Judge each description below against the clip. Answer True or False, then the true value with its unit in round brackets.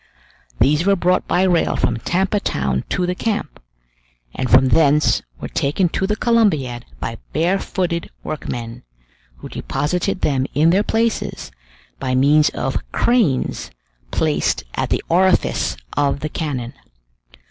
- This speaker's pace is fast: False (135 wpm)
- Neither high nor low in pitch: True (155 Hz)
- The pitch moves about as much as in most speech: False (6.2 semitones)